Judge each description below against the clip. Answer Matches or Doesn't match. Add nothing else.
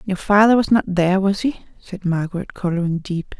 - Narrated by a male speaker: Doesn't match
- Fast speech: Doesn't match